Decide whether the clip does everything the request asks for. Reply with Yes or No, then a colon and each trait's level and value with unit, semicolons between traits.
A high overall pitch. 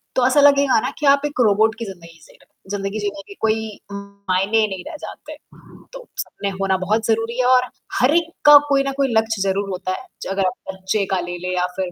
Yes: high, 215 Hz